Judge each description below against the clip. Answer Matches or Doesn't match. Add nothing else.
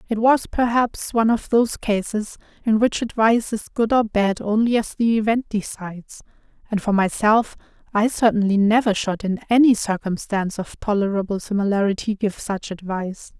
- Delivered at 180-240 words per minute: Doesn't match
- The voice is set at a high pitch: Matches